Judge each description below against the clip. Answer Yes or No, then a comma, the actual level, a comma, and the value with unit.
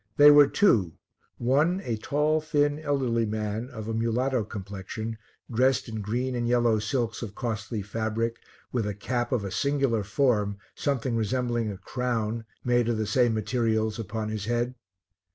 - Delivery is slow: No, average, 160 wpm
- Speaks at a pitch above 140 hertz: No, low, 115 Hz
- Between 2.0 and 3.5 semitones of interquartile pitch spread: Yes, average, 2.8 semitones